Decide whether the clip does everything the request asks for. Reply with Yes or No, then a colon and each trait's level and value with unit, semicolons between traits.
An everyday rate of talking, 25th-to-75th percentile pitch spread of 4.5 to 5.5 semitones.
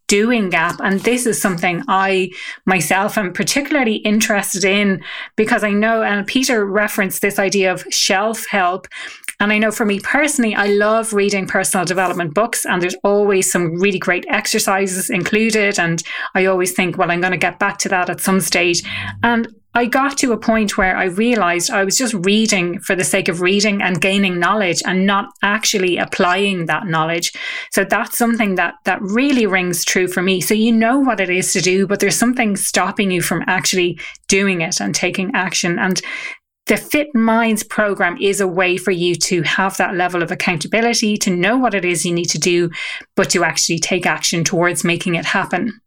No: average, 195 wpm; average, 3.0 semitones